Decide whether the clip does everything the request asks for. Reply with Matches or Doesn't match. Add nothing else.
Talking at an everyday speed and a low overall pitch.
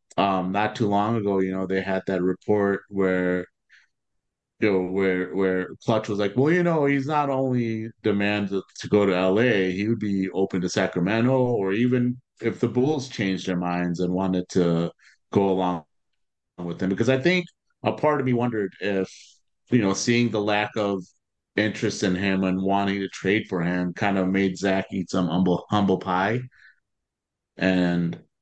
Matches